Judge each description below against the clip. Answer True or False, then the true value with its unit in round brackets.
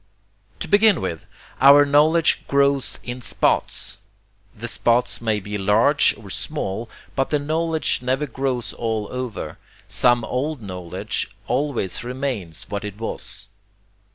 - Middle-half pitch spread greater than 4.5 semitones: True (5.3 semitones)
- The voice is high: False (125 Hz)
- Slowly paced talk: True (125 wpm)